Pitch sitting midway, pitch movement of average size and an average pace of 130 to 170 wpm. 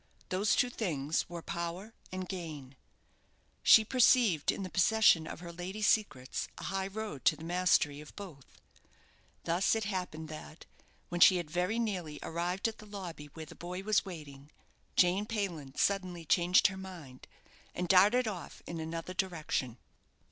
Yes: medium, 180 Hz; average, 3.7 semitones; average, 160 wpm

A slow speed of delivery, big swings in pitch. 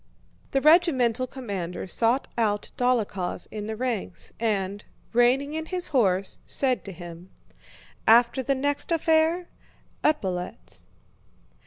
Yes: slow, 115 wpm; wide, 5.8 semitones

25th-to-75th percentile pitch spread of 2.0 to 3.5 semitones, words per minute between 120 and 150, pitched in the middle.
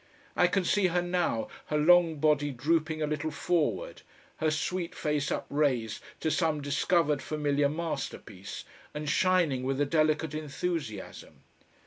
Yes: average, 2.9 semitones; slow, 135 wpm; medium, 155 Hz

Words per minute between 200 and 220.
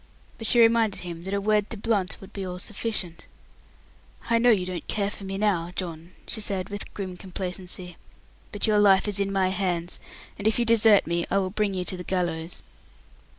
Yes: fast, 205 wpm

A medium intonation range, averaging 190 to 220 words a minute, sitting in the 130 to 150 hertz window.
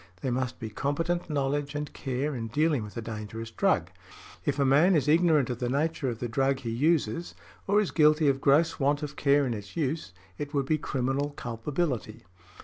Yes: average, 3.6 semitones; average, 200 wpm; medium, 140 Hz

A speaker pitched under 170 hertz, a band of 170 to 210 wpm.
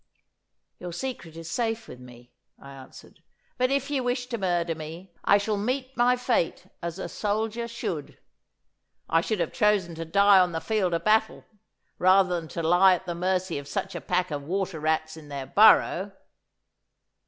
No: medium, 185 Hz; average, 180 wpm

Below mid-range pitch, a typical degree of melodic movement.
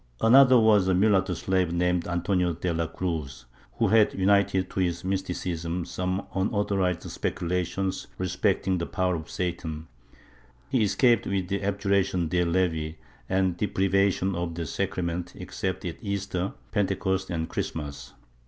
No: very low, 90 Hz; narrow, 2.1 semitones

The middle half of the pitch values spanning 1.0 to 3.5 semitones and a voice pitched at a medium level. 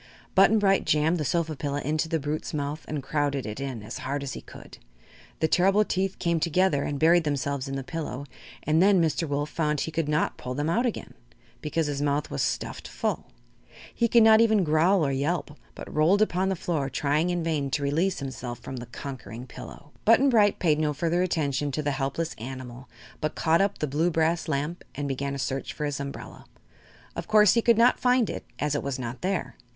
No: average, 4.1 semitones; medium, 150 Hz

